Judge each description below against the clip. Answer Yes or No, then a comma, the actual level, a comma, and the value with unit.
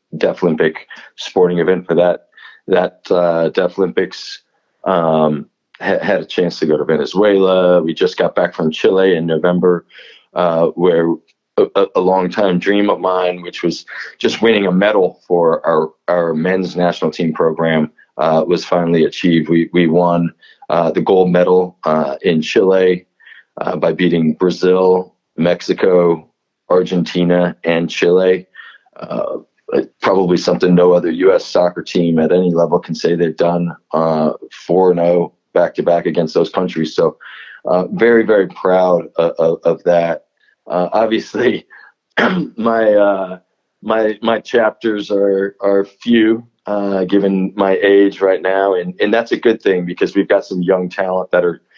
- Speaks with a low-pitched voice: Yes, very low, 90 Hz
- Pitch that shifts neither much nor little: No, narrow, 1.9 semitones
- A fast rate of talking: No, average, 150 wpm